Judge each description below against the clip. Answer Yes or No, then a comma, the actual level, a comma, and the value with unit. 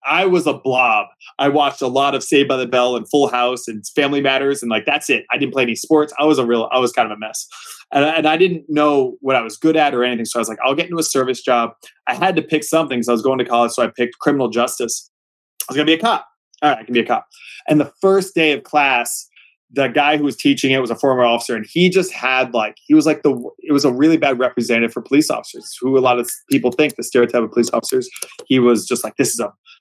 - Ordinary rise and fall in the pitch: Yes, average, 3.9 semitones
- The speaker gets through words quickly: Yes, fast, 290 wpm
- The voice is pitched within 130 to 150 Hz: Yes, low, 135 Hz